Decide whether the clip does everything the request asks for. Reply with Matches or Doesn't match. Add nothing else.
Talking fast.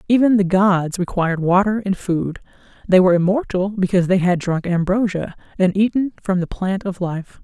Doesn't match